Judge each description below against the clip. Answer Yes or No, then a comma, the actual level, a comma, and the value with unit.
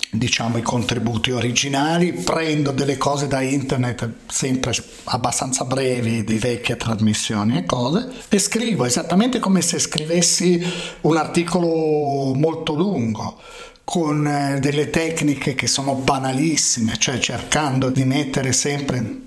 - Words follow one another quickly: No, average, 120 wpm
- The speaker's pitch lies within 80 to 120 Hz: No, medium, 140 Hz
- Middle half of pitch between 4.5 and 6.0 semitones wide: Yes, average, 4.9 semitones